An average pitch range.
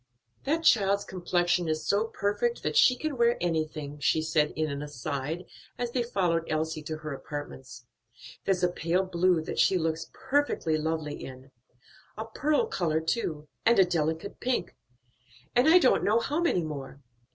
No: wide, 6.4 semitones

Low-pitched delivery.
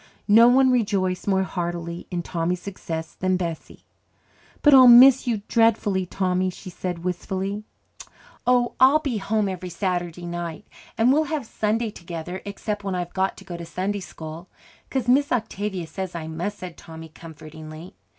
No: high, 190 Hz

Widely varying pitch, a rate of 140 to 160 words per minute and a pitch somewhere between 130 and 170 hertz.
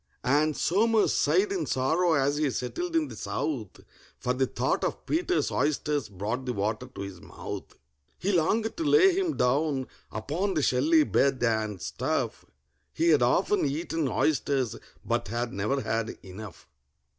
Yes: wide, 6.5 semitones; average, 155 wpm; medium, 140 Hz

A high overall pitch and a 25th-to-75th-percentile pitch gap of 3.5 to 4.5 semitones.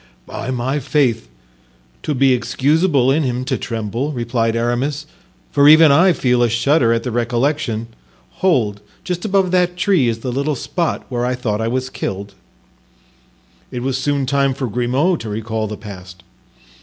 No: low, 130 Hz; average, 4.0 semitones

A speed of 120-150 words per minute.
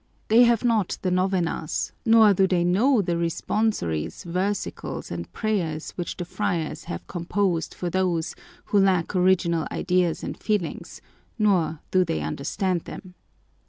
Yes: average, 140 wpm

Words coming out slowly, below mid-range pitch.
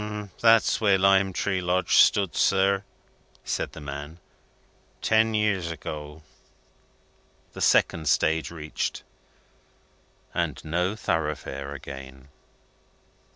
Yes: slow, 95 wpm; very low, 85 Hz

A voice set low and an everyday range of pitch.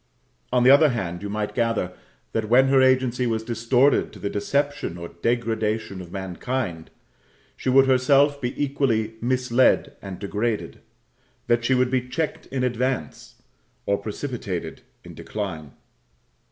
Yes: low, 120 Hz; average, 4.0 semitones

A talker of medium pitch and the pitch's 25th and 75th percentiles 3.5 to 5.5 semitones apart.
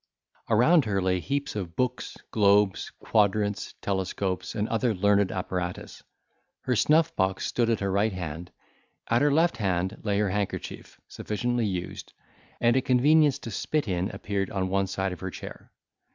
No: low, 100 Hz; average, 4.1 semitones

